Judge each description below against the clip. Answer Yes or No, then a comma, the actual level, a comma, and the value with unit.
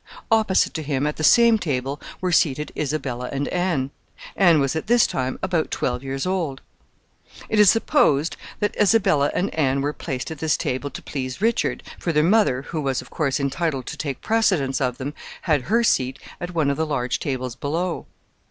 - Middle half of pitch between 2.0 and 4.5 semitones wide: No, average, 5.0 semitones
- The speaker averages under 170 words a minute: No, average, 195 wpm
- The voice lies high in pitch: No, medium, 150 Hz